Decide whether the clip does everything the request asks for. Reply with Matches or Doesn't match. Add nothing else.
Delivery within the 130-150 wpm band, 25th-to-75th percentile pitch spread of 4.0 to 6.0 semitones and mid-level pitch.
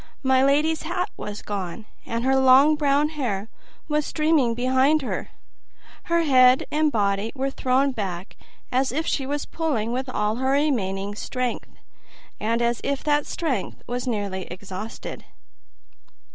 Doesn't match